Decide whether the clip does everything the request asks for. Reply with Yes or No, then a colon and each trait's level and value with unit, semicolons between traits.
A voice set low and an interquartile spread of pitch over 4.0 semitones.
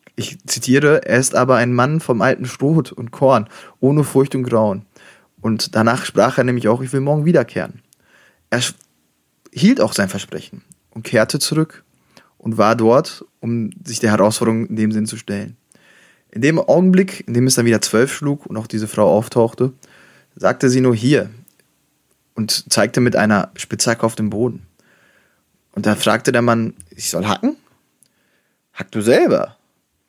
No: low, 120 Hz; average, 3.5 semitones